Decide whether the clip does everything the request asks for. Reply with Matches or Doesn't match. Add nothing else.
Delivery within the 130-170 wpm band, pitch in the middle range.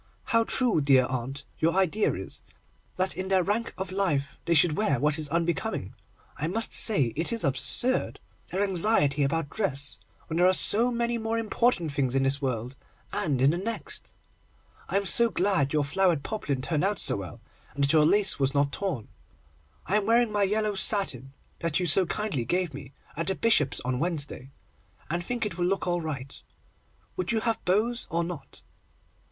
Doesn't match